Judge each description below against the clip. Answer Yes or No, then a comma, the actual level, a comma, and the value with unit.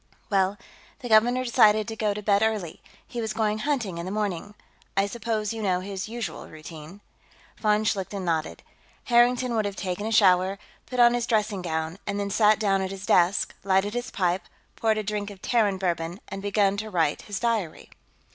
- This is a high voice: Yes, high, 205 Hz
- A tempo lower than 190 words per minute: No, average, 195 wpm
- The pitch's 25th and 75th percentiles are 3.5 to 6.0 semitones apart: No, narrow, 2.6 semitones